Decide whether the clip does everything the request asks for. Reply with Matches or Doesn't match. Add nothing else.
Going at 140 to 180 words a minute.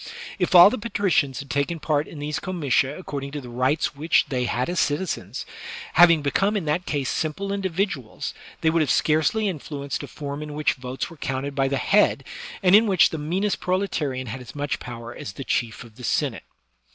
Doesn't match